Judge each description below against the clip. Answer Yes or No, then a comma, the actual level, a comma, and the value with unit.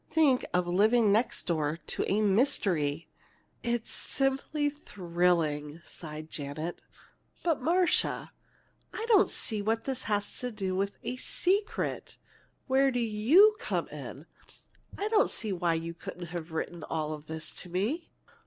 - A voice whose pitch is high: Yes, high, 205 Hz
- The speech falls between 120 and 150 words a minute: Yes, average, 145 wpm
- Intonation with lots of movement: Yes, wide, 8.0 semitones